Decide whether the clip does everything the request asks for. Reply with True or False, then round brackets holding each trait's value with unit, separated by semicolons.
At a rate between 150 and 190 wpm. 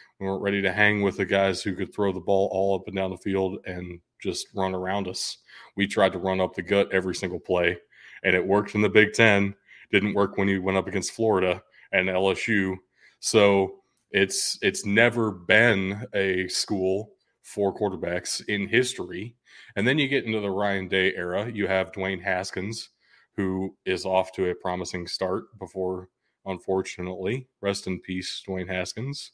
True (180 wpm)